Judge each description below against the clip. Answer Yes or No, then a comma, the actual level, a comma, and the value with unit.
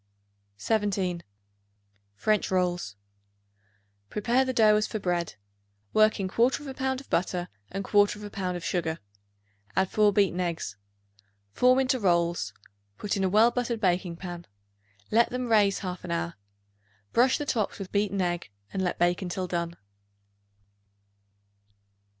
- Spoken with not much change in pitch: No, average, 3.7 semitones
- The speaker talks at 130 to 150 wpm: Yes, average, 140 wpm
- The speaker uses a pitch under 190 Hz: No, high, 195 Hz